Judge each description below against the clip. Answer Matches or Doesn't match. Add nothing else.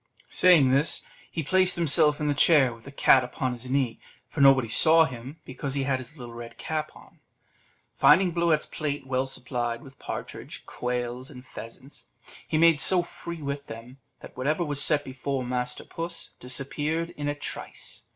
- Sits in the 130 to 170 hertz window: Matches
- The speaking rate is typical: Matches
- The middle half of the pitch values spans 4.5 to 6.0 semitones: Doesn't match